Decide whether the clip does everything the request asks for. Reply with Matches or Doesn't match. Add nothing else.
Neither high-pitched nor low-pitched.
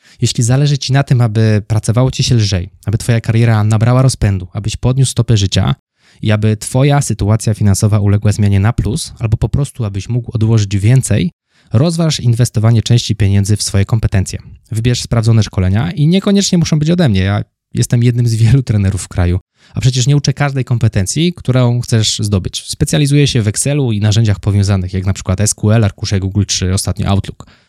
Doesn't match